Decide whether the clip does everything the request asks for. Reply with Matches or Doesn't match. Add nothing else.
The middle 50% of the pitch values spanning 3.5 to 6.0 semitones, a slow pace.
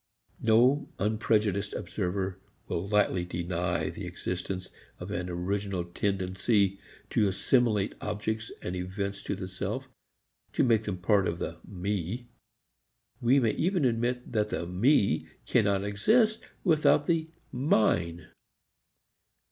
Matches